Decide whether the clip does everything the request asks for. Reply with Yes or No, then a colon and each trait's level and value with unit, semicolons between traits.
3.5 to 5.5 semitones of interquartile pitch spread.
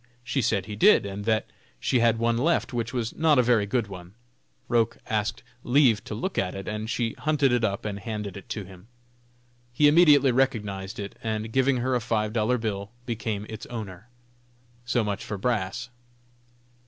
No: average, 3.1 semitones